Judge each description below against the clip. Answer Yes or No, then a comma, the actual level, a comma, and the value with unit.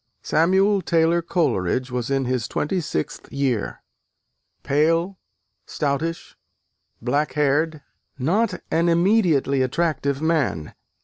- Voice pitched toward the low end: No, medium, 155 Hz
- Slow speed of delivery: Yes, slow, 100 wpm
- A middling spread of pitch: Yes, average, 3.9 semitones